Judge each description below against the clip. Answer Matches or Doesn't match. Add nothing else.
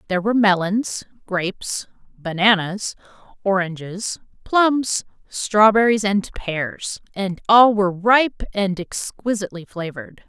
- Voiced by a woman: Matches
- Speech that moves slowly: Matches